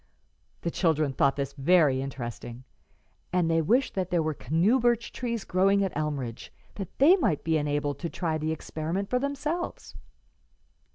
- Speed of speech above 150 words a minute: Yes, average, 160 wpm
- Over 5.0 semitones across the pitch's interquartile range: Yes, wide, 5.5 semitones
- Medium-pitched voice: Yes, medium, 165 Hz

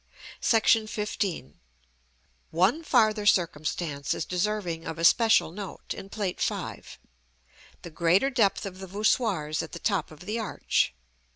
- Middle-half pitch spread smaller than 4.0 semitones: No, average, 4.4 semitones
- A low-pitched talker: No, high, 195 Hz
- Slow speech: Yes, slow, 130 wpm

